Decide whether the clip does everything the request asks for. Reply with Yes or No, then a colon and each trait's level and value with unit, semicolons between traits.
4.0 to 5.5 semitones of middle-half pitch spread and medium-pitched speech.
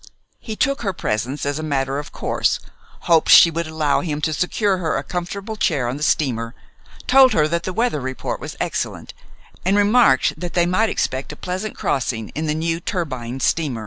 Yes: average, 5.1 semitones; medium, 160 Hz